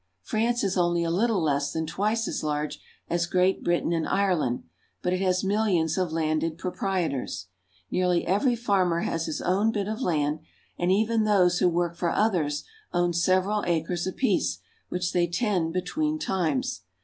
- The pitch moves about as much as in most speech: Yes, average, 3.4 semitones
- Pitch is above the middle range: No, medium, 180 Hz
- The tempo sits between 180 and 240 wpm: No, average, 165 wpm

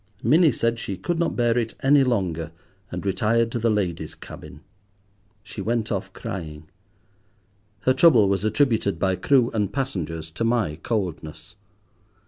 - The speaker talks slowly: No, average, 145 wpm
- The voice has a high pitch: No, low, 110 Hz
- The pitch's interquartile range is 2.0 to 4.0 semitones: No, average, 4.5 semitones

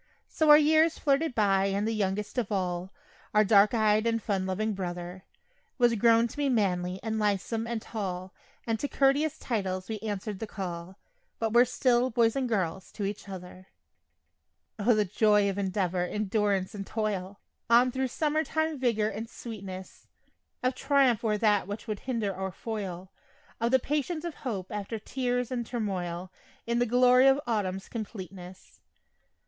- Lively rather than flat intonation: No, average, 4.1 semitones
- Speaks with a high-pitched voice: Yes, high, 215 Hz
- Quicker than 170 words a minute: No, average, 165 wpm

